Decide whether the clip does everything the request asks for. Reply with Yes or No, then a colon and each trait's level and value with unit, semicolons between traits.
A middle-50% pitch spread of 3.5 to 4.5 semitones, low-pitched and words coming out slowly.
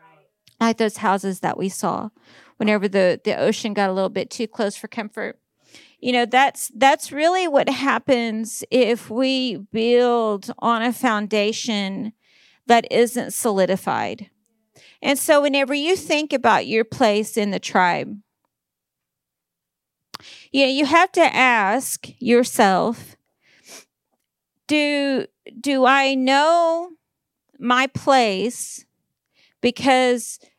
No: average, 3.9 semitones; high, 240 Hz; slow, 115 wpm